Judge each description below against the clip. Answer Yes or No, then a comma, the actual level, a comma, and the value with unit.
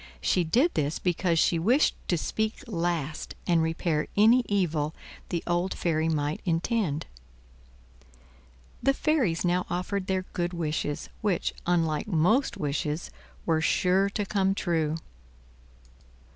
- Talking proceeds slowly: Yes, slow, 125 wpm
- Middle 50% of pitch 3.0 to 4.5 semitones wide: Yes, average, 3.7 semitones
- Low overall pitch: No, medium, 175 Hz